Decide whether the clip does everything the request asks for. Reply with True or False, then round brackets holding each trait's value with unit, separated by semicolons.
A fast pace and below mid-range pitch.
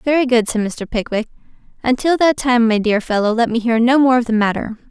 False (230 wpm; 240 Hz)